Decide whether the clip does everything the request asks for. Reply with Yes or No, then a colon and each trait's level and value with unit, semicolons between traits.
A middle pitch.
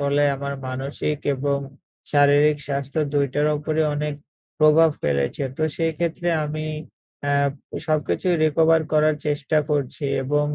Yes: medium, 150 Hz